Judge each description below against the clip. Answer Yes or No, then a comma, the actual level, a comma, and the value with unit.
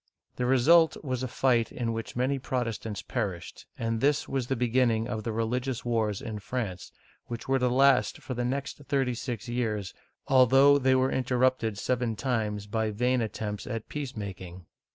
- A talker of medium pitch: No, low, 120 Hz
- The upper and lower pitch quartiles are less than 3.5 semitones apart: Yes, average, 2.8 semitones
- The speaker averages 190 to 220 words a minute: No, average, 175 wpm